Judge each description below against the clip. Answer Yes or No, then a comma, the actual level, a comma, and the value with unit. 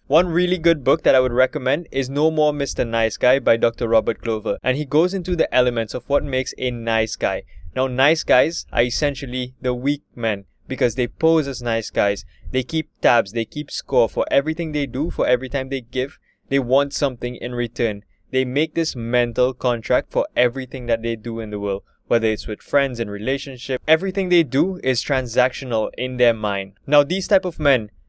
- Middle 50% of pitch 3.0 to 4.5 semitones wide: Yes, average, 3.6 semitones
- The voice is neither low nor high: No, low, 130 Hz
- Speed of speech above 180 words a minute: Yes, fast, 205 wpm